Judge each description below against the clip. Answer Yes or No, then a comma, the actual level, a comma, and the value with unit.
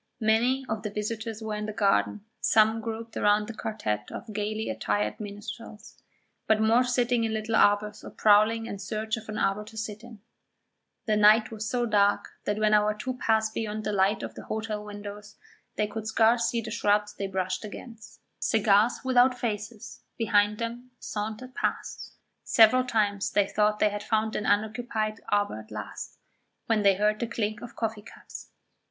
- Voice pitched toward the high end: Yes, high, 215 Hz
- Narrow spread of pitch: Yes, narrow, 1.4 semitones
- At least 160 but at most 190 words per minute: Yes, average, 180 wpm